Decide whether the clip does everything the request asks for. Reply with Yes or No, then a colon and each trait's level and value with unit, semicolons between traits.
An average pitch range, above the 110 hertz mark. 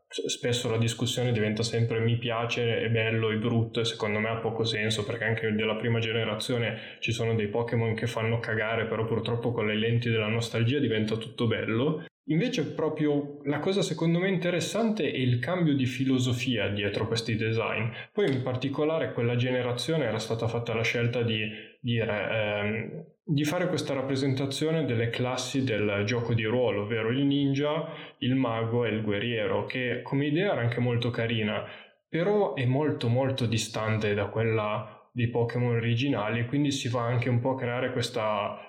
Yes: average, 3.2 semitones; low, 120 Hz